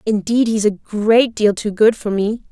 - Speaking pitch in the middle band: No, high, 215 Hz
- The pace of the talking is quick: Yes, fast, 215 wpm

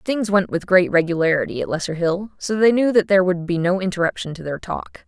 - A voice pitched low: No, medium, 185 Hz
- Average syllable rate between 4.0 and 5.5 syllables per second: No, 5.8 syllables/s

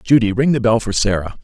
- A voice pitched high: No, low, 115 Hz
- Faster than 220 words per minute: Yes, fast, 250 wpm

